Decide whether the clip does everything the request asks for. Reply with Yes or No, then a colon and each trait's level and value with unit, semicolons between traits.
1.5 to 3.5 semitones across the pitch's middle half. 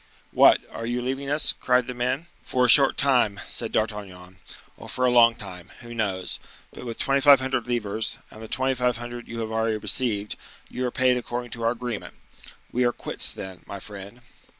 Yes: average, 2.7 semitones